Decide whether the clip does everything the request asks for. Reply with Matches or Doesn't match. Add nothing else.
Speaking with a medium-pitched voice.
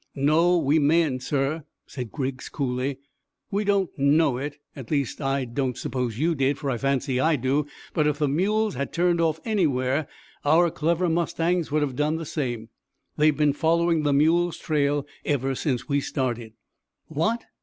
Matches